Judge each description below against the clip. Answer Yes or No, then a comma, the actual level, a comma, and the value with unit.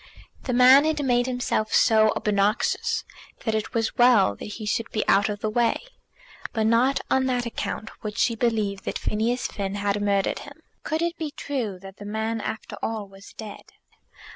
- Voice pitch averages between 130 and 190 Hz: No, high, 225 Hz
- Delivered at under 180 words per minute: No, average, 185 wpm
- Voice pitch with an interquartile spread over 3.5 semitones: No, average, 3.1 semitones